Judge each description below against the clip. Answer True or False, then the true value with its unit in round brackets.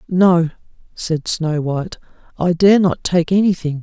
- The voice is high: False (170 Hz)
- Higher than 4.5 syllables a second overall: False (4.2 syllables/s)